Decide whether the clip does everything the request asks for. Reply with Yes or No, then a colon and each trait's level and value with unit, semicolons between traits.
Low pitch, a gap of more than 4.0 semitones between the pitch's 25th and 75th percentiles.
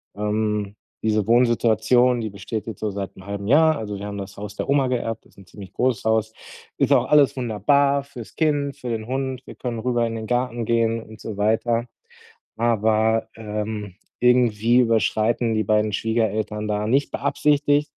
No: low, 115 Hz; average, 2.7 semitones